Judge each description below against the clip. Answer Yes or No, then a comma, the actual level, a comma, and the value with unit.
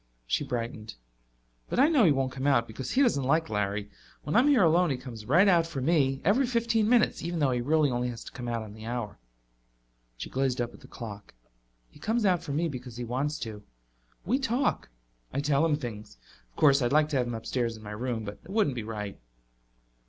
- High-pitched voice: No, low, 135 Hz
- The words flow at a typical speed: No, fast, 225 wpm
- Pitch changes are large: Yes, wide, 6.3 semitones